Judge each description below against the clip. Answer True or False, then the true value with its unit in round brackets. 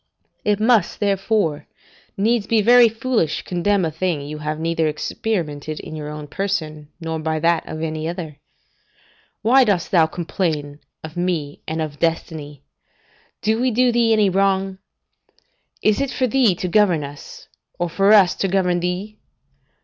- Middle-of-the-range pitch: True (175 Hz)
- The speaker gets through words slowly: False (160 wpm)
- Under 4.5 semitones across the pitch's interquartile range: False (5.0 semitones)